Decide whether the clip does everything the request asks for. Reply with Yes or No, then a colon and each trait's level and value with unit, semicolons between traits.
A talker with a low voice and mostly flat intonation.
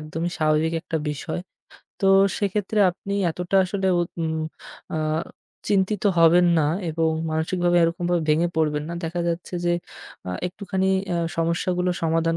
No: medium, 170 Hz; narrow, 2.0 semitones